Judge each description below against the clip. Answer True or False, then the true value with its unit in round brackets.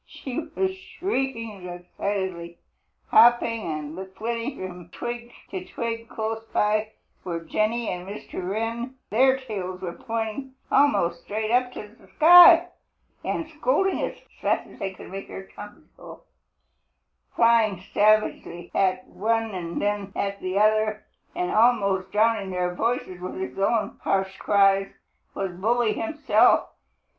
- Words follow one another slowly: True (130 wpm)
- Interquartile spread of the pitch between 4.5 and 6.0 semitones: False (3.8 semitones)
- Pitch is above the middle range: True (215 Hz)